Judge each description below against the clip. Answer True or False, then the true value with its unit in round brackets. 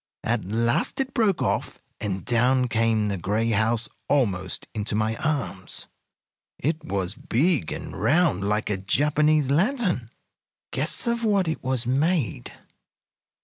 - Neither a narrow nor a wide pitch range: False (6.5 semitones)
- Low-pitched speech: True (125 Hz)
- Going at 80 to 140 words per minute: True (135 wpm)